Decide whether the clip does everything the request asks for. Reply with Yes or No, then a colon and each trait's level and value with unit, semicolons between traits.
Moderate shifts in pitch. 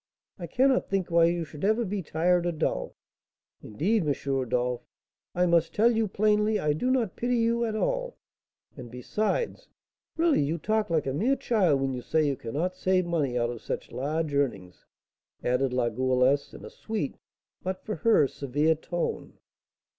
No: wide, 7.9 semitones